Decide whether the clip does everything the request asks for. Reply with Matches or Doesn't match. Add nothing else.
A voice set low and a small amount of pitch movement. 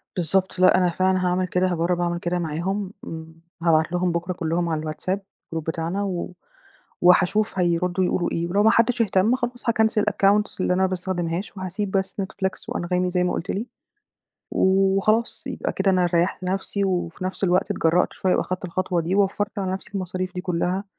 Doesn't match